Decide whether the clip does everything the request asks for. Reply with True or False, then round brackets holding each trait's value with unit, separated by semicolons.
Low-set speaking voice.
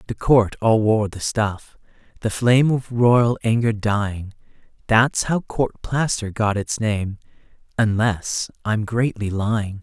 True (110 Hz)